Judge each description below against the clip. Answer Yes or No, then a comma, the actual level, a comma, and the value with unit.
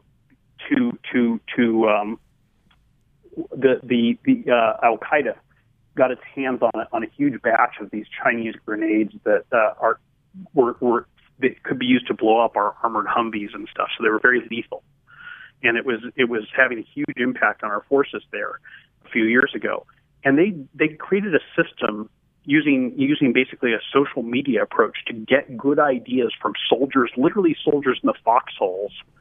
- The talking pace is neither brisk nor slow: Yes, average, 175 wpm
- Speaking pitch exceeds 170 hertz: No, medium, 140 Hz